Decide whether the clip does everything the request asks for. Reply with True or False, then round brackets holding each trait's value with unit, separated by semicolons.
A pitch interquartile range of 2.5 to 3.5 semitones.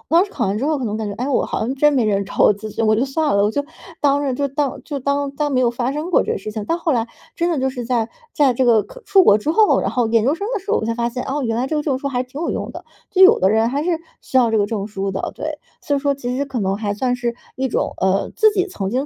False (4.7 semitones)